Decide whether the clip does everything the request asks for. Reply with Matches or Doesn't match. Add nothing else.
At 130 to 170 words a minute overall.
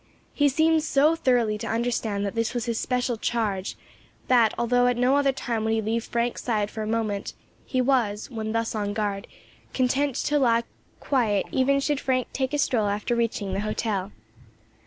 Doesn't match